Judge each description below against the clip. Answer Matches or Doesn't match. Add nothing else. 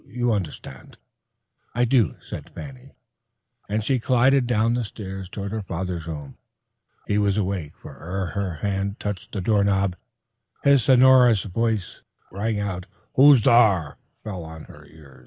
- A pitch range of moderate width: Matches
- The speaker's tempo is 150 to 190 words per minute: Doesn't match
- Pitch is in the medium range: Doesn't match